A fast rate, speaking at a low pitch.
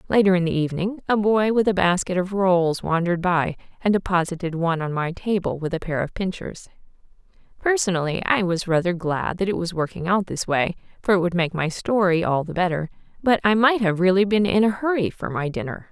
No: fast, 215 wpm; medium, 185 Hz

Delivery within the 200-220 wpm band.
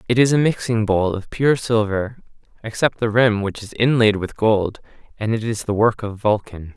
Yes: fast, 205 wpm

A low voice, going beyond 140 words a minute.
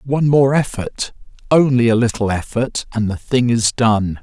Yes: low, 120 Hz; average, 170 wpm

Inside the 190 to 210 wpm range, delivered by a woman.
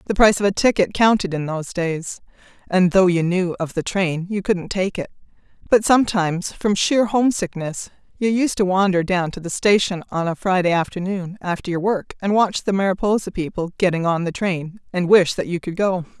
Yes: fast, 205 wpm; female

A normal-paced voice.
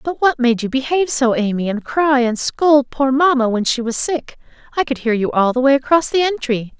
No: fast, 240 wpm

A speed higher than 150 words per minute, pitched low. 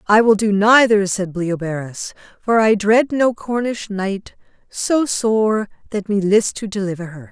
No: average, 165 wpm; high, 205 Hz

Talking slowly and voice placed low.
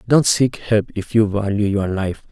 No: fast, 205 wpm; low, 105 Hz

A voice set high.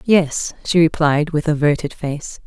No: medium, 155 Hz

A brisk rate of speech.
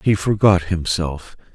No: slow, 115 wpm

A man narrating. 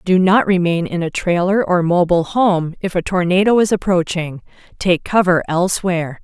No: female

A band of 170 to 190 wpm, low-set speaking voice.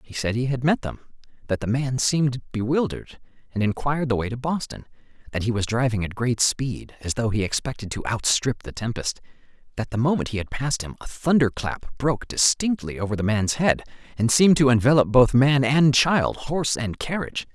No: average, 200 wpm; low, 125 Hz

